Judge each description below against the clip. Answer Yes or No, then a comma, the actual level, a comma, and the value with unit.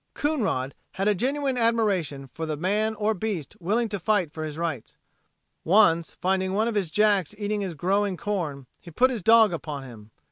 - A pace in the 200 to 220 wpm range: No, average, 185 wpm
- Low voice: No, high, 195 Hz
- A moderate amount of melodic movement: Yes, average, 5.0 semitones